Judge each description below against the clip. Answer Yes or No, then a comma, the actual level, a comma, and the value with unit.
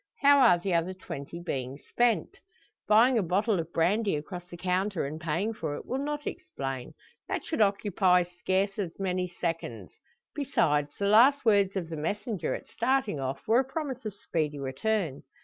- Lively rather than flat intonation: No, average, 5.0 semitones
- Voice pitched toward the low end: No, medium, 185 Hz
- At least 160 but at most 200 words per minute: Yes, average, 175 wpm